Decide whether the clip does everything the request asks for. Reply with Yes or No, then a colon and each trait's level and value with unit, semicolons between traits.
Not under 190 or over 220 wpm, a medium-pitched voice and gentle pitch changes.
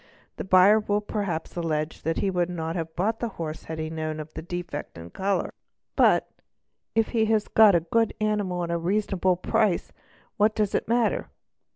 No: average, 200 wpm; medium, 180 Hz; average, 4.5 semitones